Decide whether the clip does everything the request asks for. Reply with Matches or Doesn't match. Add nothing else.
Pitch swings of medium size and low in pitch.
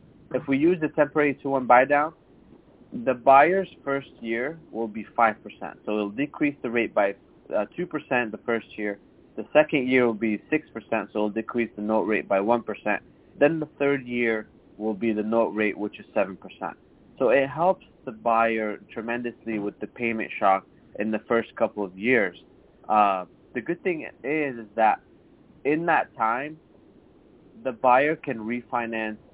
Matches